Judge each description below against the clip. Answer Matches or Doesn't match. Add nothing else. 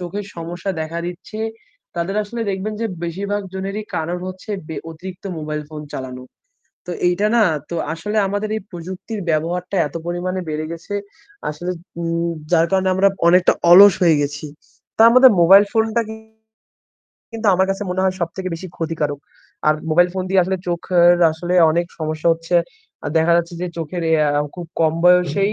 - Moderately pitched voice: Matches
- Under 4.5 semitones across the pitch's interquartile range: Matches